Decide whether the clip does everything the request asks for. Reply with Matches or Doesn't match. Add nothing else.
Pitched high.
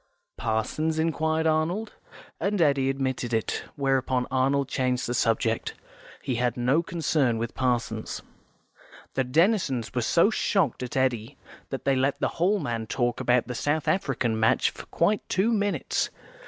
Doesn't match